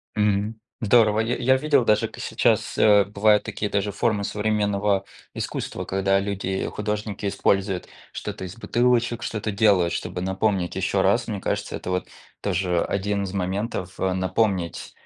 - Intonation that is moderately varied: No, narrow, 2.1 semitones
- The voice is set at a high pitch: No, low, 100 Hz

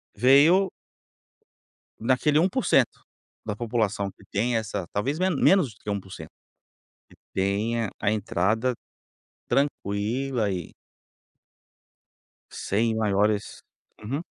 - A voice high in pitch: No, low, 110 Hz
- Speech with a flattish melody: No, average, 4.9 semitones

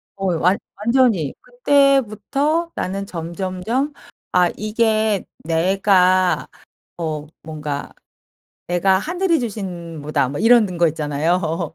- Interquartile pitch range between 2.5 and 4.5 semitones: No, wide, 5.5 semitones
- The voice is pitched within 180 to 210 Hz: Yes, high, 190 Hz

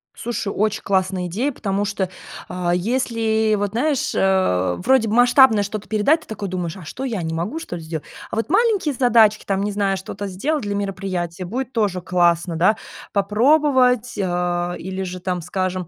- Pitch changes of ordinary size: Yes, average, 4.3 semitones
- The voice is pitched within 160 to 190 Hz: No, high, 200 Hz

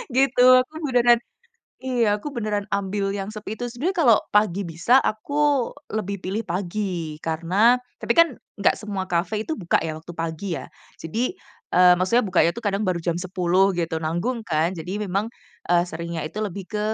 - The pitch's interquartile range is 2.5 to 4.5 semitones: No, average, 4.9 semitones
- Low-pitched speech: No, high, 200 Hz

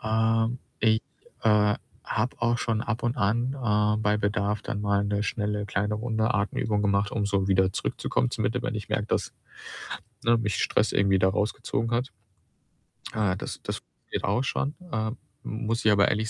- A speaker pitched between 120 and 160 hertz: No, low, 105 Hz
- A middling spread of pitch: No, narrow, 1.9 semitones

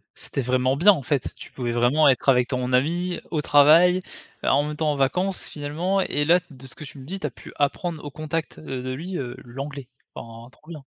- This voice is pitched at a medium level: Yes, medium, 145 Hz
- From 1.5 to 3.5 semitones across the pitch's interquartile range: No, average, 4.0 semitones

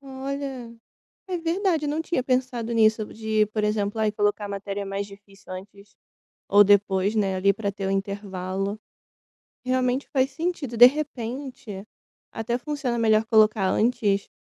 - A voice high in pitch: Yes, high, 220 Hz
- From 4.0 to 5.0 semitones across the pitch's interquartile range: Yes, average, 4.3 semitones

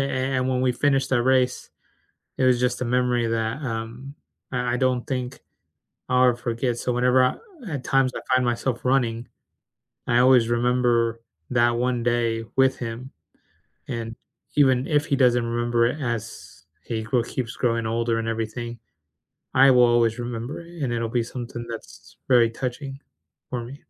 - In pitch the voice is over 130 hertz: No, low, 125 Hz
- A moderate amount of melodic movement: No, narrow, 1.6 semitones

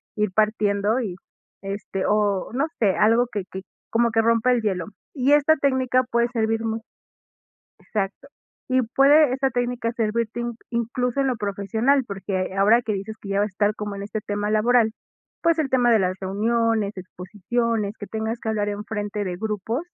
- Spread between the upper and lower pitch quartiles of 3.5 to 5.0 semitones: No, average, 2.9 semitones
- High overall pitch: Yes, high, 220 Hz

